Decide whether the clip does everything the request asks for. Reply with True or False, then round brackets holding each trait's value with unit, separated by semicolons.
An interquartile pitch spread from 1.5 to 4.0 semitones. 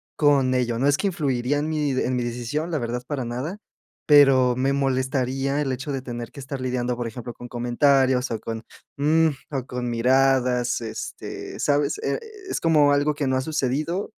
True (2.9 semitones)